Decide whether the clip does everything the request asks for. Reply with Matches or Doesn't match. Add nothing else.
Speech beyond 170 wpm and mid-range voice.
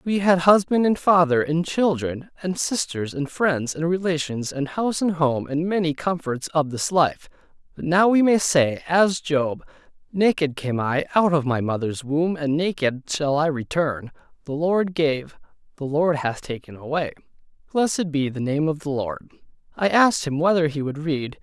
Matches